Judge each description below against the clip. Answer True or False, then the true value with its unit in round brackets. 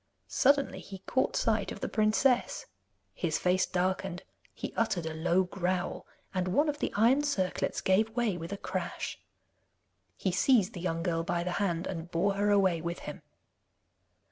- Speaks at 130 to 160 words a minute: False (170 wpm)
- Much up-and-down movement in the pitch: False (3.5 semitones)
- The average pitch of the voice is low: False (185 Hz)